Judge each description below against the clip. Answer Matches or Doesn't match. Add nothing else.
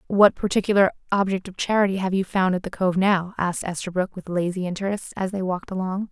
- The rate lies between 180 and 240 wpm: Matches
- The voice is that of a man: Doesn't match